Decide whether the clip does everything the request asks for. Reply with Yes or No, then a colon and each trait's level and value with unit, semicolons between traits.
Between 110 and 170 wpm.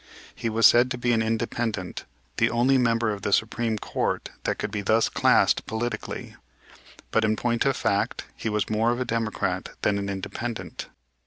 No: average, 180 wpm